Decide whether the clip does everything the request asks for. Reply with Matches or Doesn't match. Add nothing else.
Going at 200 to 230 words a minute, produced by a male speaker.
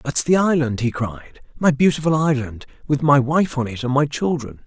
Matches